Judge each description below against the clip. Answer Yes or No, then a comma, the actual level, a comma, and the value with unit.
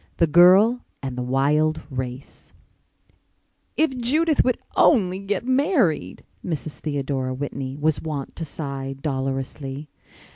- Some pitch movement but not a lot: No, wide, 6.5 semitones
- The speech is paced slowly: Yes, slow, 115 wpm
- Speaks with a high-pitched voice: No, medium, 150 Hz